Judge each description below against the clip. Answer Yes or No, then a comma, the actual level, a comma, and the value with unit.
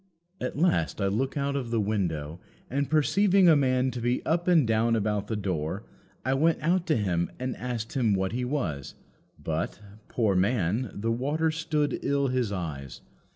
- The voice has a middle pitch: No, low, 120 Hz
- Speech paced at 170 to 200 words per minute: Yes, average, 180 wpm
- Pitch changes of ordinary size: No, wide, 6.0 semitones